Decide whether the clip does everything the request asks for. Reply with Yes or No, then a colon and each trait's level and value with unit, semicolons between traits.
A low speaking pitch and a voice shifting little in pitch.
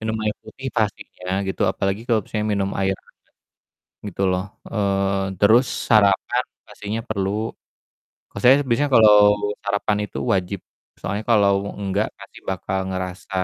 Yes: low, 100 Hz; narrow, 2.2 semitones